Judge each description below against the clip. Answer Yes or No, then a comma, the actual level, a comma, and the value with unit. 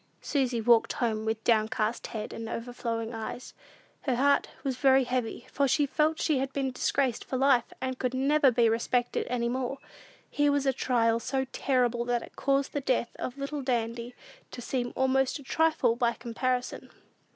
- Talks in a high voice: Yes, very high, 255 Hz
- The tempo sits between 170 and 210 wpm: Yes, average, 175 wpm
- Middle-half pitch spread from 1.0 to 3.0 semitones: Yes, narrow, 2.5 semitones